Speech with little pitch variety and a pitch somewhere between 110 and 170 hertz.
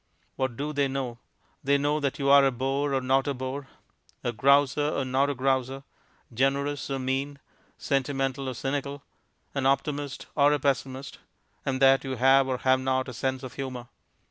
Yes: narrow, 1.3 semitones; low, 135 Hz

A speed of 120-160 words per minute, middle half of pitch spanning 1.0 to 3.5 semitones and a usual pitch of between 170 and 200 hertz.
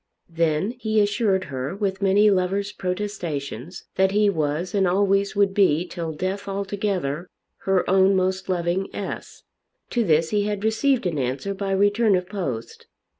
Yes: average, 155 wpm; average, 2.9 semitones; high, 190 Hz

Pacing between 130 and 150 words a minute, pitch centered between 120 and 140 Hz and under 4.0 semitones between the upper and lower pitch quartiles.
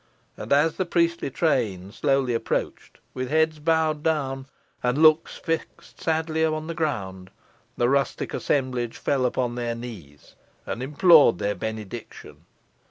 No: slow, 135 wpm; low, 135 Hz; average, 5.0 semitones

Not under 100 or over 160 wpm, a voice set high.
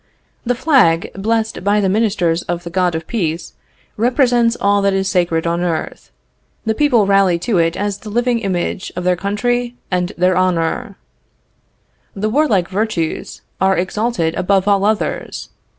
Yes: average, 155 wpm; high, 195 Hz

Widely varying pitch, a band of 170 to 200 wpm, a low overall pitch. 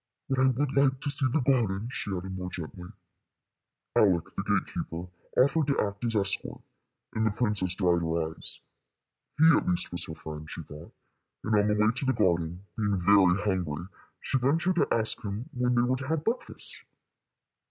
Yes: wide, 6.6 semitones; average, 190 wpm; low, 105 Hz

